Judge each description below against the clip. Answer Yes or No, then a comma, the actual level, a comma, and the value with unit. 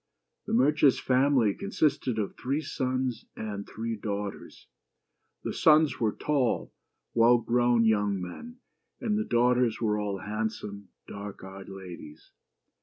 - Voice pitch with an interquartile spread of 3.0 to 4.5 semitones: Yes, average, 4.2 semitones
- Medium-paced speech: No, slow, 125 wpm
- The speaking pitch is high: No, low, 115 Hz